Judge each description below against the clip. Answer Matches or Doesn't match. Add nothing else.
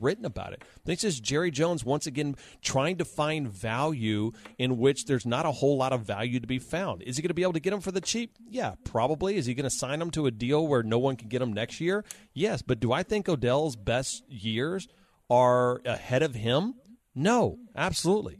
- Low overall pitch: Doesn't match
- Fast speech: Matches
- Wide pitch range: Matches